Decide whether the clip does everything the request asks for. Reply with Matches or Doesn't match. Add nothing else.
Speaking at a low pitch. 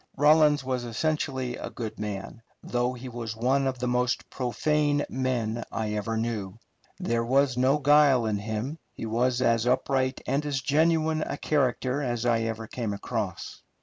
Matches